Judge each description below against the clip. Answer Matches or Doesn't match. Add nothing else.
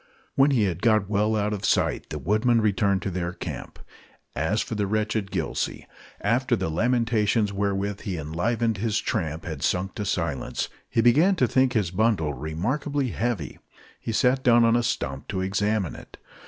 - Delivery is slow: Doesn't match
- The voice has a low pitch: Matches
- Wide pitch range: Doesn't match